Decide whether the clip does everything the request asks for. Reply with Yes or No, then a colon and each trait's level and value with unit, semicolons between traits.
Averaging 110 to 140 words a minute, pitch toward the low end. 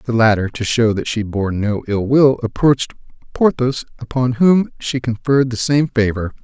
No: average, 175 wpm; low, 120 Hz